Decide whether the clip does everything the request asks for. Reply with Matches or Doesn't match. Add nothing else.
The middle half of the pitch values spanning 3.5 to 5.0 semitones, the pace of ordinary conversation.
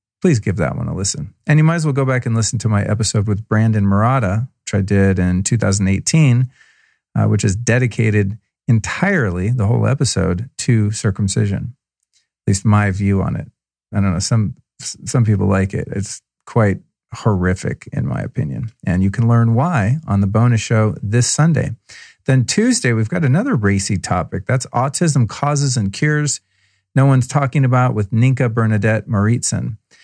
Matches